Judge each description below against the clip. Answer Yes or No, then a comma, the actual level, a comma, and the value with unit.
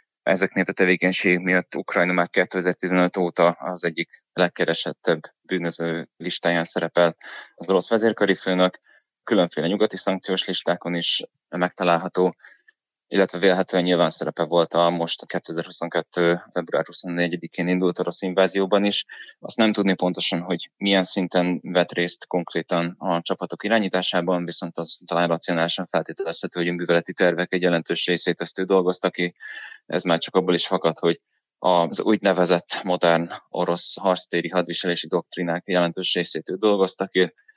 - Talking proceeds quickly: No, average, 140 wpm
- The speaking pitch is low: Yes, very low, 90 Hz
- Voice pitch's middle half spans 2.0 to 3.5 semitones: No, narrow, 1.5 semitones